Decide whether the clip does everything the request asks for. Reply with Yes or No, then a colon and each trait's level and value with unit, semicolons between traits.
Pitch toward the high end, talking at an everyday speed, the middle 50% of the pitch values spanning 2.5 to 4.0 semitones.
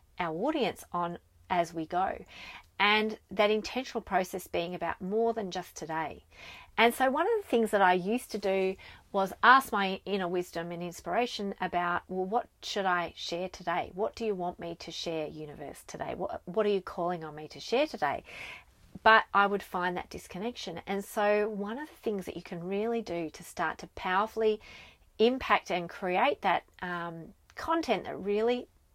Yes: high, 195 Hz; average, 185 wpm; average, 3.7 semitones